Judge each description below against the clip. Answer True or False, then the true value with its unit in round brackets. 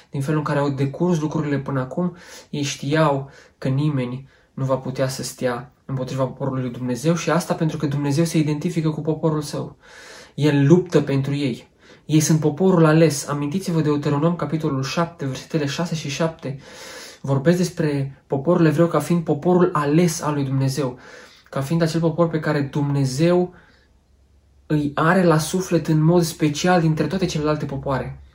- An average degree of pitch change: True (3.4 semitones)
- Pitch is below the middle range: False (150 Hz)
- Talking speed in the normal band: True (165 wpm)